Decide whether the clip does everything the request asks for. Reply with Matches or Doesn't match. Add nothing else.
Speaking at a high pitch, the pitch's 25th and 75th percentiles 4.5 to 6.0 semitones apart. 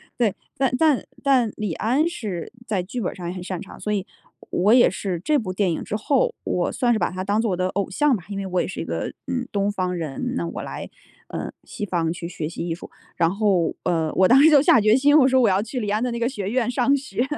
Matches